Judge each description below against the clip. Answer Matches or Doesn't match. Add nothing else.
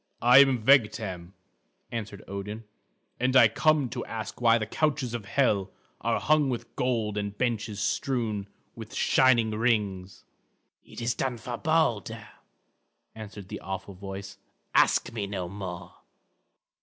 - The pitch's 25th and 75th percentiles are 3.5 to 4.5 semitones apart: Matches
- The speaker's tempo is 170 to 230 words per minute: Doesn't match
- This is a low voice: Matches